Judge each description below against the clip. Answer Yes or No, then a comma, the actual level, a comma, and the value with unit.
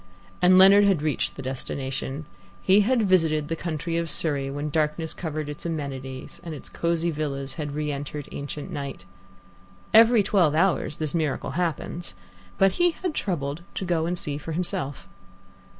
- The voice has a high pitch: No, medium, 155 Hz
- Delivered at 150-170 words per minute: Yes, average, 165 wpm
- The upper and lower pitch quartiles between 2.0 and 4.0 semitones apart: Yes, average, 3.7 semitones